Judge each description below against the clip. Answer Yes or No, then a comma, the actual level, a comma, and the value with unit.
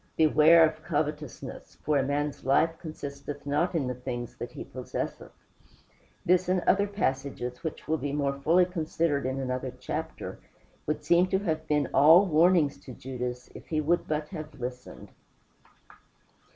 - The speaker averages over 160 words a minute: No, average, 155 wpm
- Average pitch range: Yes, average, 3.2 semitones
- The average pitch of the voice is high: No, medium, 150 Hz